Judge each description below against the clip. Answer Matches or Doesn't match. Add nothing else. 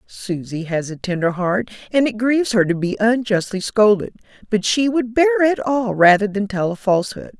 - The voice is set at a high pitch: Matches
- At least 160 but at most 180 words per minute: Doesn't match